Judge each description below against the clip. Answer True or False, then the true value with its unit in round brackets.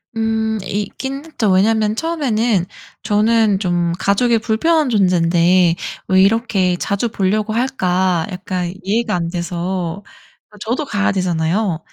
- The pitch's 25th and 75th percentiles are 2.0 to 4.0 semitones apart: True (3.7 semitones)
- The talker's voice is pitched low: False (205 Hz)